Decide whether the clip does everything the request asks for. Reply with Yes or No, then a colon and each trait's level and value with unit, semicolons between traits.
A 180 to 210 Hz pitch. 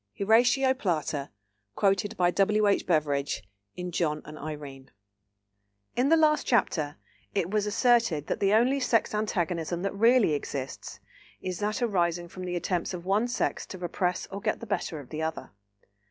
Yes: medium, 185 Hz